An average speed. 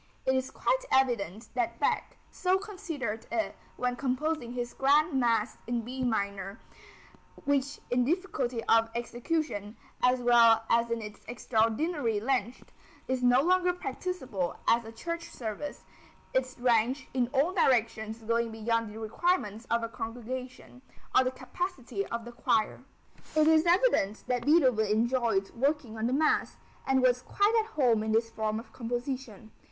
Yes: average, 150 wpm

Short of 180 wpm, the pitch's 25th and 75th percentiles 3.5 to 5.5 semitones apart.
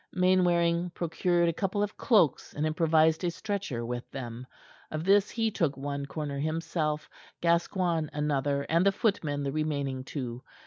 Yes: average, 150 wpm; average, 3.9 semitones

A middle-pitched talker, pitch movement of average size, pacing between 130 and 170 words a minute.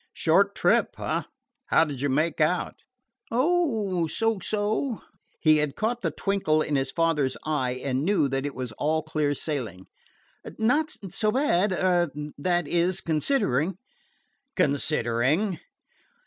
No: medium, 160 Hz; wide, 6.3 semitones; slow, 135 wpm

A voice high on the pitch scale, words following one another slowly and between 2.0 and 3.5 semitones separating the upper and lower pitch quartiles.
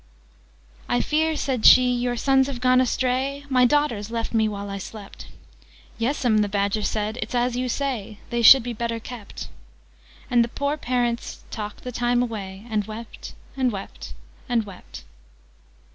No: high, 240 Hz; average, 165 wpm; average, 2.9 semitones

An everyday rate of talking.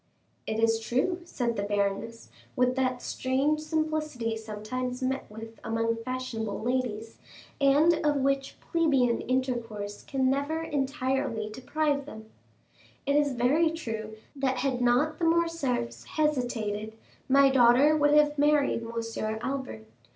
No: slow, 125 wpm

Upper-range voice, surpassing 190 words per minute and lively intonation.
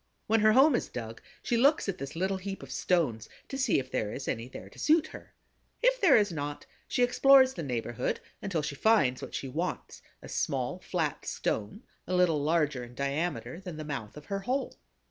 No: medium, 170 Hz; fast, 205 wpm; wide, 8.4 semitones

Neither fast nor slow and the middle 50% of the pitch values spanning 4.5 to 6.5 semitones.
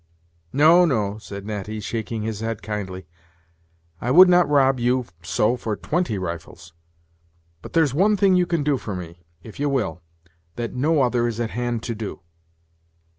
Yes: average, 170 wpm; wide, 5.6 semitones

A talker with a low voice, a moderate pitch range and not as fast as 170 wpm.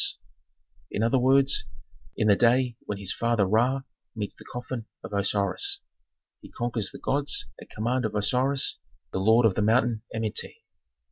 Yes: low, 115 Hz; average, 3.4 semitones; average, 155 wpm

